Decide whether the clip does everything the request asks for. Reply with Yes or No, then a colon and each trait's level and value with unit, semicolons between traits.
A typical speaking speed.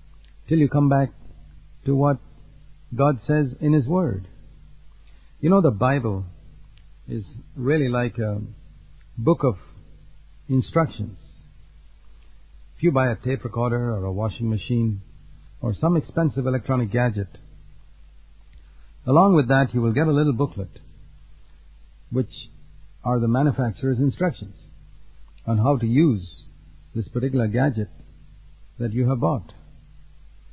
No: slow, 120 wpm